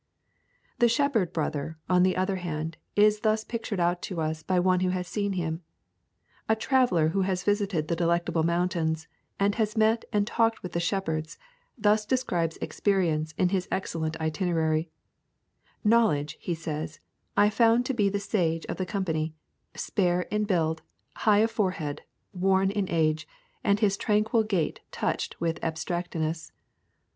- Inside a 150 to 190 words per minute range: Yes, average, 155 wpm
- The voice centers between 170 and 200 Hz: Yes, medium, 185 Hz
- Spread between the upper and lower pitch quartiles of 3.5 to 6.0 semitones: Yes, average, 4.3 semitones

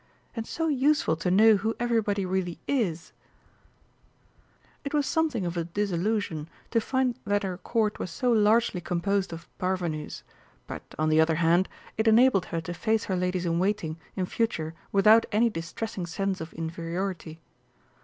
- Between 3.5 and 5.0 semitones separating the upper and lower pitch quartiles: Yes, average, 4.7 semitones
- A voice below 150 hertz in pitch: No, high, 190 Hz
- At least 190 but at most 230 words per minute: No, average, 160 wpm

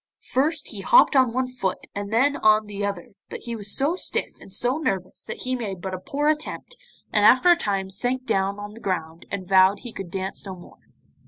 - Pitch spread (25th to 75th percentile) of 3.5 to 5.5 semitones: Yes, average, 5.1 semitones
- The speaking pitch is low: No, high, 205 Hz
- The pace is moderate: No, fast, 225 wpm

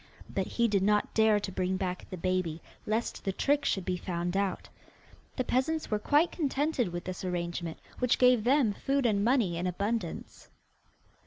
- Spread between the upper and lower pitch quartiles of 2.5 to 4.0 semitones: No, wide, 5.4 semitones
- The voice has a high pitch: Yes, high, 205 Hz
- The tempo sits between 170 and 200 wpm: Yes, average, 175 wpm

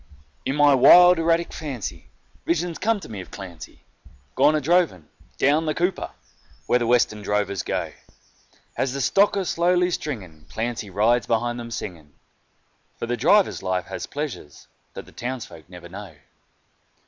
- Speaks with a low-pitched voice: Yes, low, 125 Hz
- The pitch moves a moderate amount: No, wide, 8.4 semitones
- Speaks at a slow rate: No, average, 155 wpm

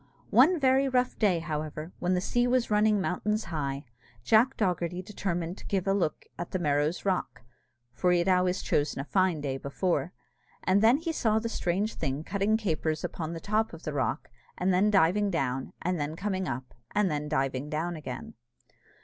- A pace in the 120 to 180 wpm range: No, average, 190 wpm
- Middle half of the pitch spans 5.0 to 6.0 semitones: Yes, wide, 5.4 semitones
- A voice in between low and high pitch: Yes, medium, 180 Hz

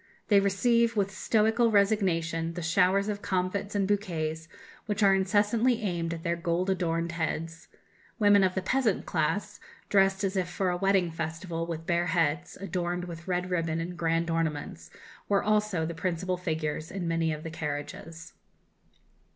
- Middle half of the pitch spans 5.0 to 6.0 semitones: No, average, 3.2 semitones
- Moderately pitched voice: Yes, medium, 180 Hz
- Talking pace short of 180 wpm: Yes, average, 160 wpm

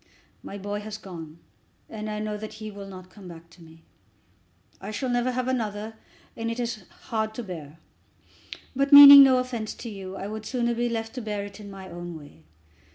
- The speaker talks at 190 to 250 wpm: Yes, fast, 205 wpm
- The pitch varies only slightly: No, average, 3.7 semitones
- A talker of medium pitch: No, high, 215 Hz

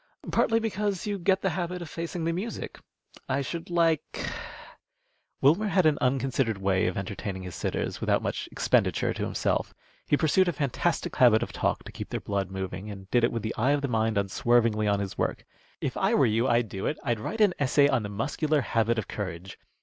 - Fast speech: Yes, fast, 210 wpm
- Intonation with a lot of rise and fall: Yes, wide, 8.2 semitones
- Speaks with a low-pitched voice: Yes, low, 130 Hz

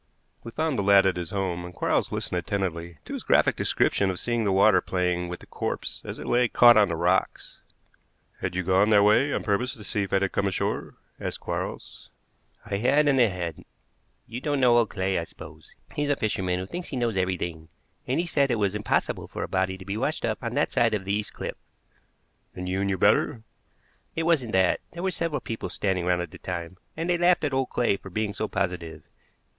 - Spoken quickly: Yes, fast, 225 wpm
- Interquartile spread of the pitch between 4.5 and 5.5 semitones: Yes, average, 4.8 semitones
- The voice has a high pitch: No, low, 100 Hz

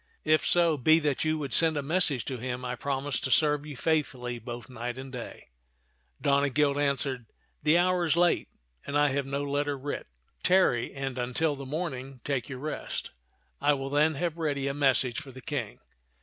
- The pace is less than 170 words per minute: No, average, 190 wpm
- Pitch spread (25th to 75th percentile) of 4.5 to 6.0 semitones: No, average, 2.7 semitones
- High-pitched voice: No, medium, 140 Hz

